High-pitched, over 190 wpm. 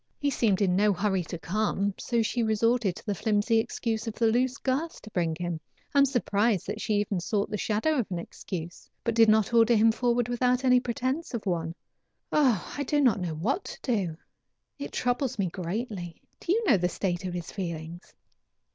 Yes: high, 215 Hz; average, 200 wpm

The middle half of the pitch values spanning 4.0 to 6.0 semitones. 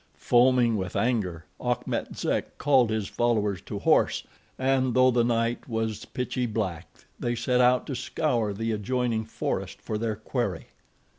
No: narrow, 2.5 semitones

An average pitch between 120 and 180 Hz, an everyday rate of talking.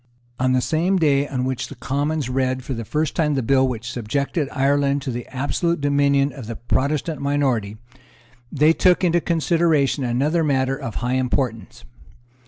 Yes: medium, 140 Hz; average, 170 wpm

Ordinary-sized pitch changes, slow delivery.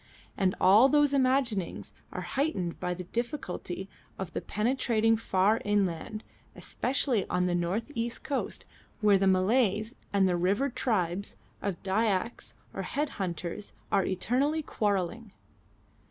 Yes: average, 4.5 semitones; slow, 125 wpm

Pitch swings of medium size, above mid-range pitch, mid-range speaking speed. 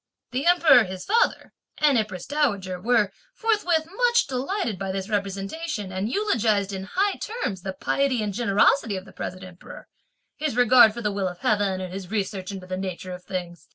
No: wide, 6.2 semitones; high, 205 Hz; average, 185 wpm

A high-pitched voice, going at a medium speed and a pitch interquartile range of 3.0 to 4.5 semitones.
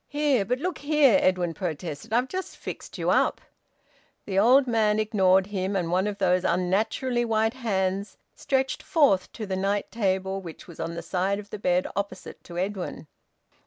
Yes: high, 200 Hz; average, 180 wpm; average, 3.9 semitones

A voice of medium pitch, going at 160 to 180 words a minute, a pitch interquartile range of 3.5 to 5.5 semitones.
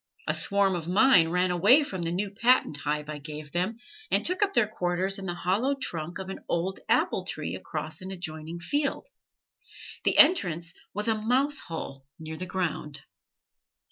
Yes: medium, 180 Hz; average, 175 wpm; average, 4.8 semitones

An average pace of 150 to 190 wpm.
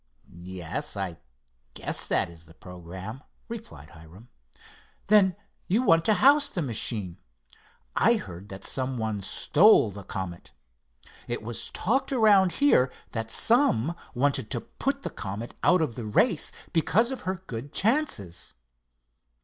No: average, 140 wpm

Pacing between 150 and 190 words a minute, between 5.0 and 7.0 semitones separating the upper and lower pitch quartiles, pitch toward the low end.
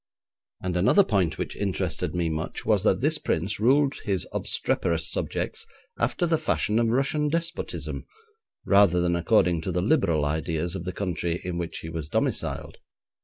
Yes: average, 165 wpm; average, 5.3 semitones; very low, 90 Hz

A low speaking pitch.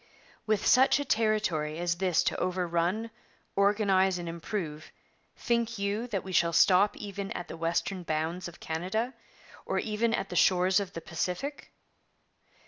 No: high, 190 Hz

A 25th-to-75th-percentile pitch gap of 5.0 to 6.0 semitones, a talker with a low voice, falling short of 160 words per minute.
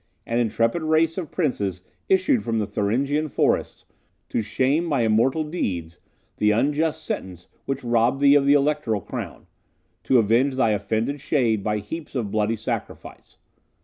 Yes: wide, 5.4 semitones; low, 120 Hz; average, 150 wpm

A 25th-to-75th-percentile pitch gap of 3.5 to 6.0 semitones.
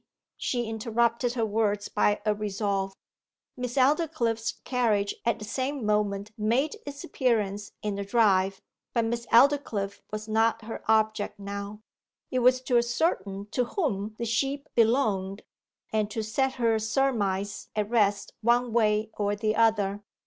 No: average, 2.8 semitones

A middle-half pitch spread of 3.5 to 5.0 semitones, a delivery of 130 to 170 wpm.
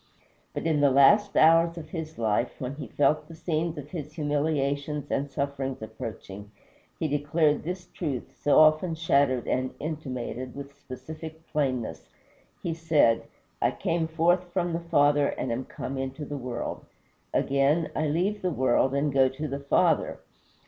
No: average, 3.1 semitones; average, 160 wpm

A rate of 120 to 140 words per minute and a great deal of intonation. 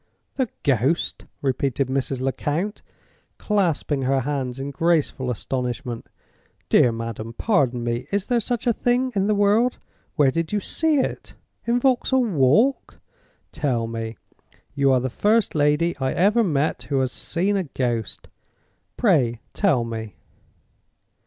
Yes: slow, 135 wpm; wide, 8.3 semitones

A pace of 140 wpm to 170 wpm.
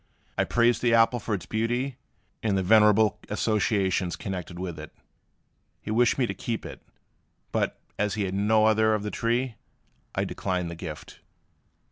Yes: average, 165 wpm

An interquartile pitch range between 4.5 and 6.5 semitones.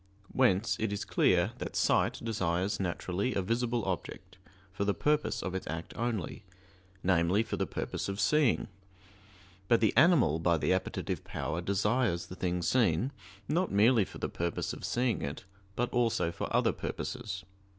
Yes: average, 4.9 semitones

